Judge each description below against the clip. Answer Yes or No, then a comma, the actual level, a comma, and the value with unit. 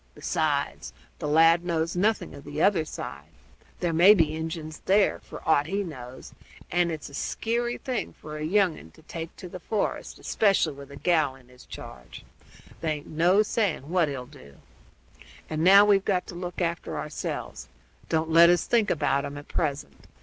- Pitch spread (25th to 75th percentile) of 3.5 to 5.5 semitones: Yes, average, 3.8 semitones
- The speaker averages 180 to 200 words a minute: Yes, average, 185 wpm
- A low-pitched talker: No, medium, 165 Hz